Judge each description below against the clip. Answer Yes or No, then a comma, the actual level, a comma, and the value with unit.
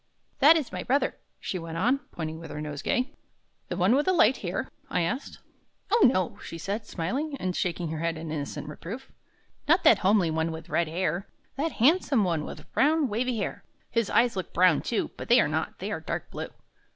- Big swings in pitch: Yes, wide, 7.6 semitones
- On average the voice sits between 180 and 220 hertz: Yes, high, 190 Hz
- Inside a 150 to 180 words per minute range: No, fast, 205 wpm